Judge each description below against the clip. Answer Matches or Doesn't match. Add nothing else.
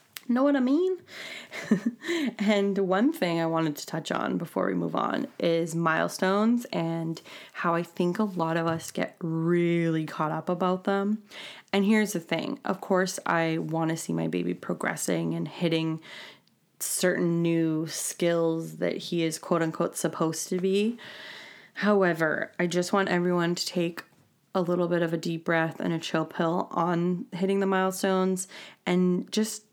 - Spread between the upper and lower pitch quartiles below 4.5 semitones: Matches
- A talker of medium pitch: Matches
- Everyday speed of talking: Matches